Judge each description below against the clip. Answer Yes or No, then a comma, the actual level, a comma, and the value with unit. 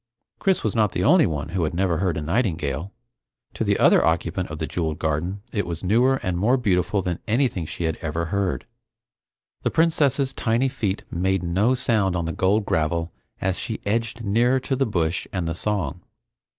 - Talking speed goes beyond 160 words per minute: Yes, average, 190 wpm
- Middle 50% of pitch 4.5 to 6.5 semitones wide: Yes, average, 5.3 semitones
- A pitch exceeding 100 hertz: No, very low, 95 Hz